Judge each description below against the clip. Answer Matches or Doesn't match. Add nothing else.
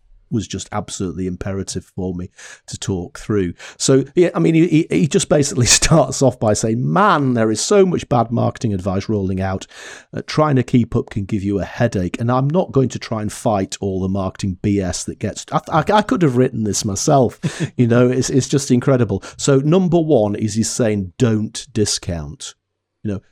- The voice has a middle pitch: Doesn't match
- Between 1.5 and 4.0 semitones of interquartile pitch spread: Doesn't match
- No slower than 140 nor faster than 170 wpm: Doesn't match